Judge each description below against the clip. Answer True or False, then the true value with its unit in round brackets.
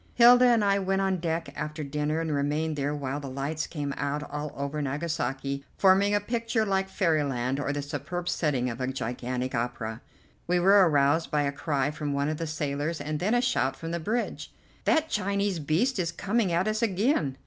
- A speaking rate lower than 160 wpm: False (200 wpm)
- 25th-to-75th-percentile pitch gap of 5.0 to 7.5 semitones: True (5.3 semitones)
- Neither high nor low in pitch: True (155 Hz)